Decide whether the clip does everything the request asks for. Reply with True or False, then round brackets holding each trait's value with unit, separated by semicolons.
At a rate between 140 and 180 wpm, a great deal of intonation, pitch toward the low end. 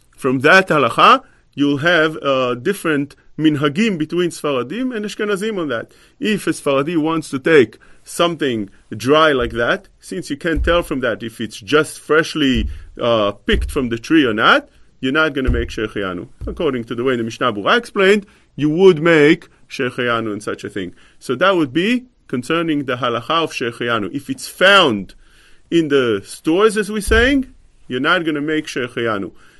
False (175 wpm; 6.2 semitones; 150 Hz)